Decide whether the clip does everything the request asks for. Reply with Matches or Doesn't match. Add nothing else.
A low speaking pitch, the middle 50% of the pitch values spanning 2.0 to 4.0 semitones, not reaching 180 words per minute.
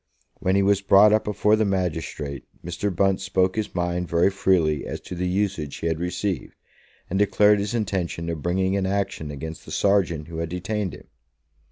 Doesn't match